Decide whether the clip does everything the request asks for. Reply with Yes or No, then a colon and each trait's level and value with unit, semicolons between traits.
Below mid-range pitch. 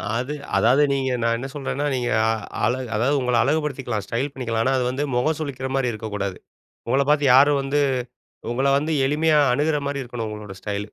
Yes: low, 130 Hz